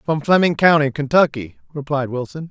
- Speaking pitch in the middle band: Yes, medium, 145 Hz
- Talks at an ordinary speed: Yes, average, 145 wpm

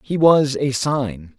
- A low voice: Yes, low, 130 Hz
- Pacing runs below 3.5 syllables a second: Yes, 3.2 syllables/s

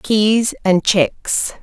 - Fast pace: No, slow, 110 wpm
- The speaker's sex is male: No, female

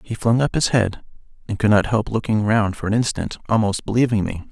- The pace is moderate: No, fast, 225 wpm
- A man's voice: Yes, male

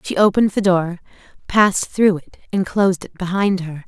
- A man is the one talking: No, female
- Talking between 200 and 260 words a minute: No, average, 185 wpm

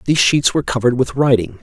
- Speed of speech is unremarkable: No, fast, 220 wpm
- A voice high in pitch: No, low, 125 Hz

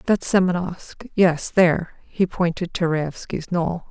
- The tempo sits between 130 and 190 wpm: Yes, average, 140 wpm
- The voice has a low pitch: No, medium, 175 Hz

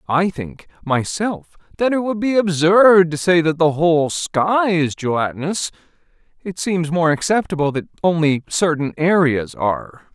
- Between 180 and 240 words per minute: No, average, 150 wpm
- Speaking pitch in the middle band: Yes, medium, 165 Hz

